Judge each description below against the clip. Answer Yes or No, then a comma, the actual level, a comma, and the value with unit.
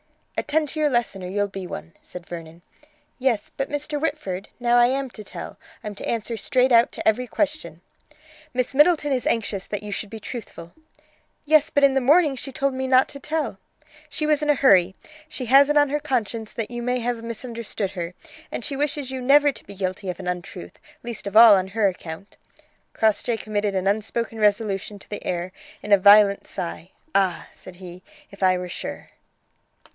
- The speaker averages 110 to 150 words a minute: No, average, 200 wpm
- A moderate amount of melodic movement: No, wide, 5.7 semitones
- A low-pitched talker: No, high, 225 Hz